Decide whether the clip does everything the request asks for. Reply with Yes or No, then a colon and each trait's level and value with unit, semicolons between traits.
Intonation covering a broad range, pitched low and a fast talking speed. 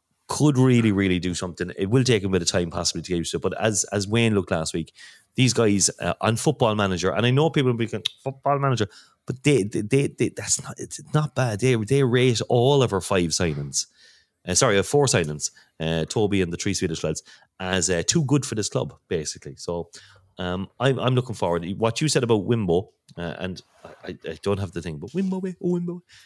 Yes: wide, 6.3 semitones; low, 110 Hz; fast, 230 wpm